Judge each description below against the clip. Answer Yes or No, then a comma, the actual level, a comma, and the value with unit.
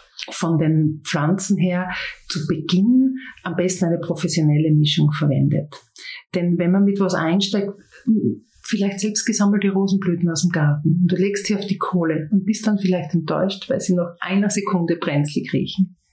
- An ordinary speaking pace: Yes, average, 165 wpm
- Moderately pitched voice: Yes, medium, 180 Hz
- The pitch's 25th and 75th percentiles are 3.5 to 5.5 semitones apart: No, average, 3.0 semitones